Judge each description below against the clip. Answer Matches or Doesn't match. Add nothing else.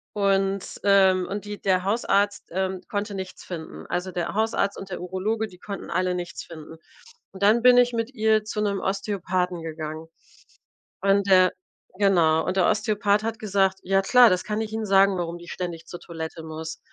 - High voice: Matches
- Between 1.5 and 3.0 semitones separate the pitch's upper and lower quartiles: Matches